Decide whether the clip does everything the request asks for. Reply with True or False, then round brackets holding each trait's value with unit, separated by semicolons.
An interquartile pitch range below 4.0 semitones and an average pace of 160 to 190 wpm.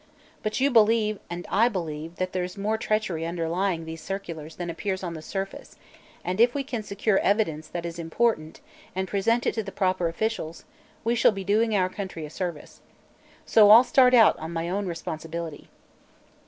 False (4.4 semitones; 180 wpm)